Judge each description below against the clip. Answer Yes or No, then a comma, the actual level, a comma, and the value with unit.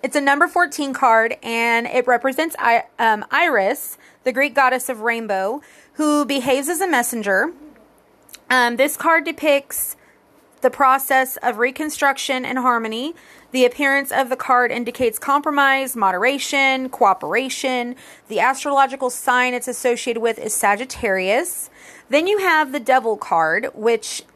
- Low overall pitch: No, very high, 260 Hz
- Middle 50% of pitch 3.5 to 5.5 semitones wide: No, average, 2.8 semitones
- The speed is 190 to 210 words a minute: No, average, 140 wpm